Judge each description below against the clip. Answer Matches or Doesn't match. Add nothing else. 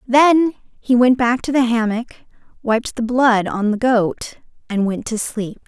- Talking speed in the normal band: Matches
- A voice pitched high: Matches